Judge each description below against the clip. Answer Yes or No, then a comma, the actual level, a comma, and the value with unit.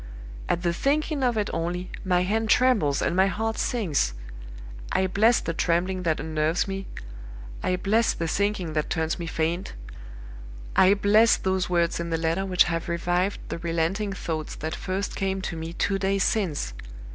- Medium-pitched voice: Yes, medium, 180 Hz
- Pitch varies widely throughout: No, average, 3.3 semitones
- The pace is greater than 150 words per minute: Yes, average, 170 wpm